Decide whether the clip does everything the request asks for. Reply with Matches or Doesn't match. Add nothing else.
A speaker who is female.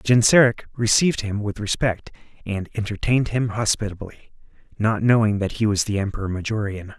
Doesn't match